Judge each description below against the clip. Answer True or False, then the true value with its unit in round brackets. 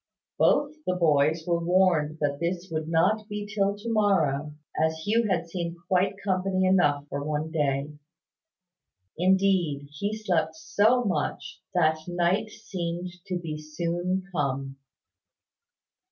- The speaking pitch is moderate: True (175 Hz)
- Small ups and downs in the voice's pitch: False (3.8 semitones)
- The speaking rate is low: True (130 wpm)